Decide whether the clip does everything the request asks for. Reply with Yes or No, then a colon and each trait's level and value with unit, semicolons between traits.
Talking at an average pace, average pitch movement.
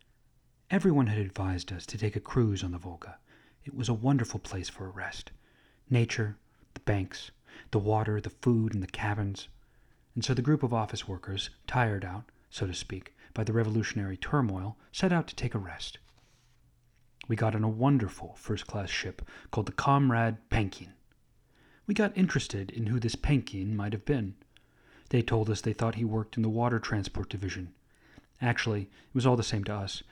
Yes: average, 185 wpm; average, 3.4 semitones